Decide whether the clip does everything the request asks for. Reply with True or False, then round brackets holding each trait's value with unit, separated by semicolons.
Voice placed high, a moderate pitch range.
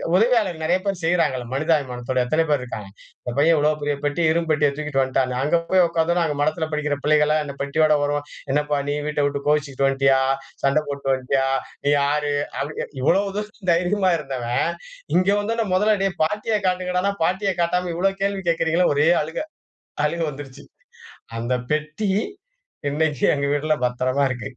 False (150 Hz; 4.0 semitones)